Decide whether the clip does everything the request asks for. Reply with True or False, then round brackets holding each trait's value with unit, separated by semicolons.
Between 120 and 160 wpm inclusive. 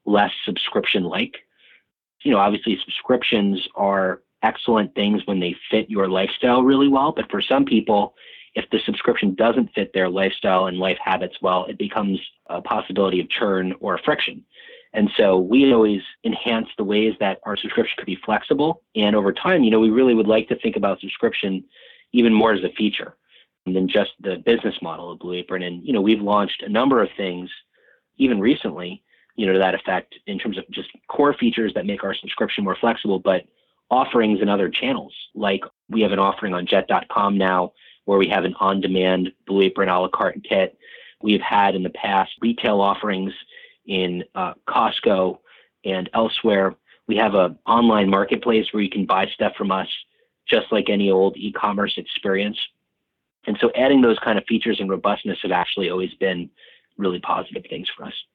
False (185 wpm)